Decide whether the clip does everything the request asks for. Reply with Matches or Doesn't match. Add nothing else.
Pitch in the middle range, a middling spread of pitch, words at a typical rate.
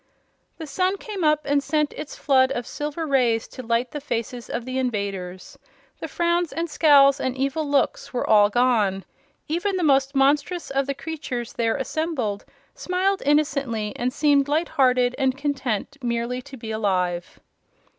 Doesn't match